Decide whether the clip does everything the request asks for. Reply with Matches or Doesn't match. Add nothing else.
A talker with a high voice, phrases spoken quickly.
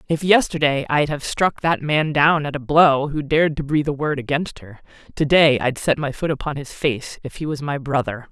Doesn't match